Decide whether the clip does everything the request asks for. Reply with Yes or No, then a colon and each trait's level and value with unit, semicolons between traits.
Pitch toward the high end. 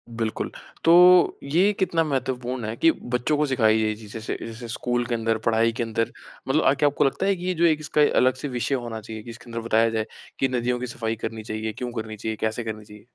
No: low, 120 Hz